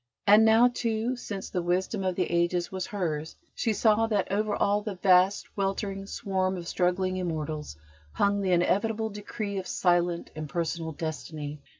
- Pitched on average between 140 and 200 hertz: Yes, high, 190 Hz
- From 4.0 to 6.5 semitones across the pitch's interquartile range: No, average, 3.1 semitones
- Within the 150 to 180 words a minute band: Yes, average, 160 wpm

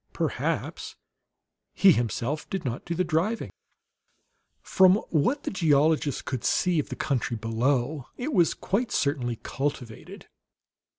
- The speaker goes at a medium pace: No, slow, 125 wpm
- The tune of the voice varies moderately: No, wide, 6.3 semitones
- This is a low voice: No, medium, 150 Hz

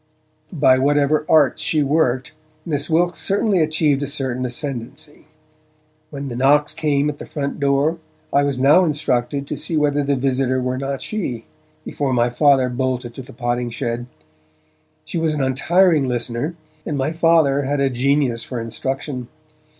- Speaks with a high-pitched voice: No, medium, 140 Hz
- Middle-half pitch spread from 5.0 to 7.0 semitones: No, average, 2.9 semitones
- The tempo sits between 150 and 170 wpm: Yes, average, 160 wpm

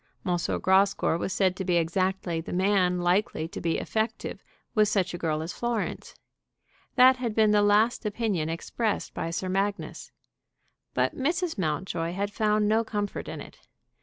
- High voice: Yes, high, 195 Hz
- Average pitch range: Yes, average, 3.4 semitones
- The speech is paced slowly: No, average, 165 wpm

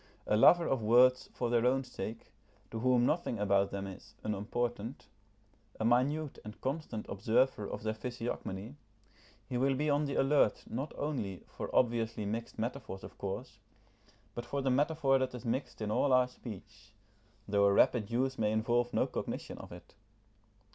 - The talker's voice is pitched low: Yes, low, 120 Hz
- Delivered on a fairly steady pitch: No, average, 3.8 semitones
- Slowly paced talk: No, average, 170 wpm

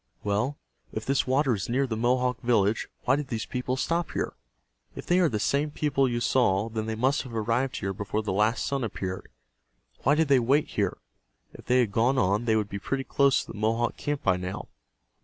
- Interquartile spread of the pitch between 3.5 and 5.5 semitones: Yes, average, 4.0 semitones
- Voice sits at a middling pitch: No, low, 120 Hz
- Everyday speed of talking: No, fast, 215 wpm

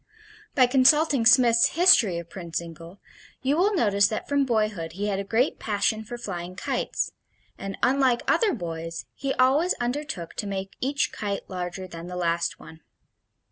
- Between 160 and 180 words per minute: Yes, average, 165 wpm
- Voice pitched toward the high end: Yes, high, 210 Hz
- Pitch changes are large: Yes, wide, 6.6 semitones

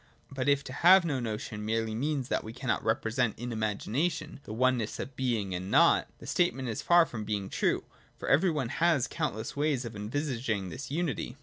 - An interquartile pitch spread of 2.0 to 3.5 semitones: No, average, 4.8 semitones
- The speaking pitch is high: No, low, 125 Hz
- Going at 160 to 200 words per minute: Yes, average, 195 wpm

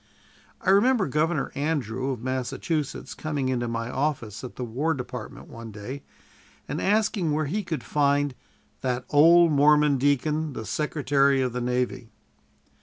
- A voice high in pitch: No, medium, 140 Hz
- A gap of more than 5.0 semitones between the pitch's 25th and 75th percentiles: No, average, 3.5 semitones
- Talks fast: No, average, 145 wpm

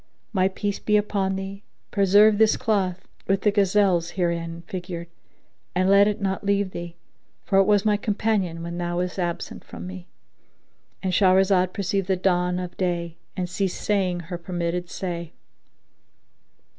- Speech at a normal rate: Yes, average, 150 wpm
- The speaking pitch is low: No, medium, 185 Hz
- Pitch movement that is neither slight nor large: No, narrow, 2.2 semitones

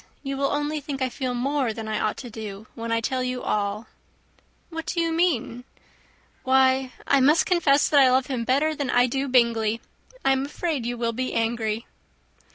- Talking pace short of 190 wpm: No, average, 195 wpm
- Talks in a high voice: Yes, very high, 255 Hz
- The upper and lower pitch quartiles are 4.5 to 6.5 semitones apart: No, average, 3.4 semitones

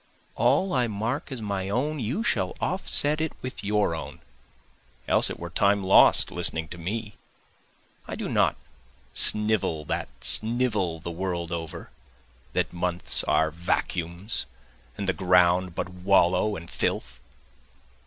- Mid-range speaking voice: No, very low, 95 Hz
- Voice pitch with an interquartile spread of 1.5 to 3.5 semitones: No, average, 4.0 semitones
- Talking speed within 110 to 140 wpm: Yes, slow, 135 wpm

